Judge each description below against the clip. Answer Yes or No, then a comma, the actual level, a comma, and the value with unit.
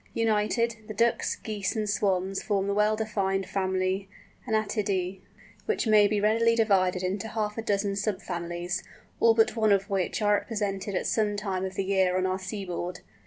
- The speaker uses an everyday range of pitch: No, narrow, 2.3 semitones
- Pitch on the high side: Yes, high, 200 Hz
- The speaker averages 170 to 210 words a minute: Yes, average, 175 wpm